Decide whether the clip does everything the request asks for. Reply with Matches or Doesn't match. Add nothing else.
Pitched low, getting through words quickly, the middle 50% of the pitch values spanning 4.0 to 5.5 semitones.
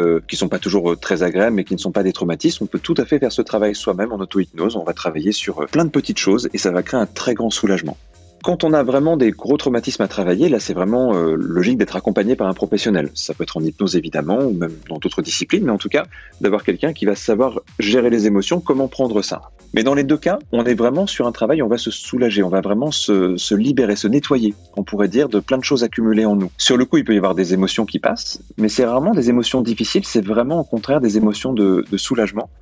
Matches